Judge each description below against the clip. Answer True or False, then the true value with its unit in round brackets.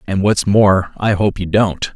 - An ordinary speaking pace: False (215 wpm)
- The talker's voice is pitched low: True (95 Hz)